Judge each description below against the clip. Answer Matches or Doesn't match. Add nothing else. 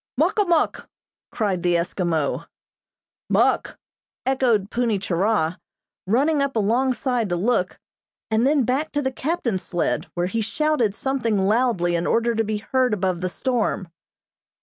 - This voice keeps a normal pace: Matches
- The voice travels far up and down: Matches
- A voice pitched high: Matches